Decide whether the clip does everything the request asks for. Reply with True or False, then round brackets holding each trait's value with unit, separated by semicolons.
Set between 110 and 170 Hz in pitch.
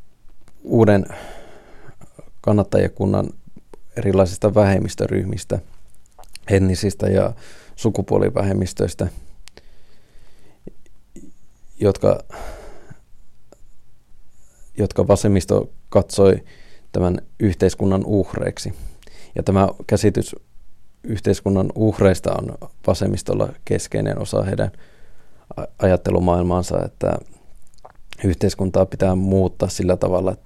False (95 Hz)